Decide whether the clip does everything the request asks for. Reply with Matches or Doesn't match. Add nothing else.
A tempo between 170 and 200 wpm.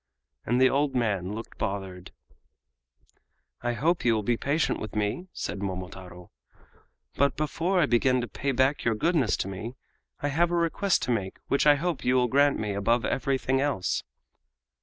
Matches